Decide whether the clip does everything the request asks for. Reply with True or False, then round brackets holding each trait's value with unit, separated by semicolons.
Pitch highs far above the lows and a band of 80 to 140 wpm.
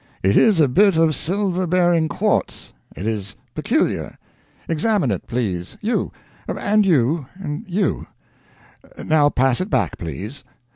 True (7.2 semitones; 135 wpm)